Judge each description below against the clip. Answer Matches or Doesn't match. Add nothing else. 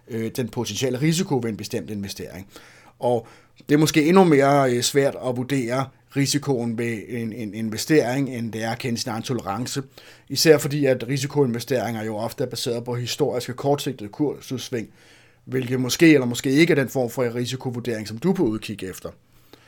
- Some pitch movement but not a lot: Matches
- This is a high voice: Doesn't match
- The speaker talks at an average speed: Matches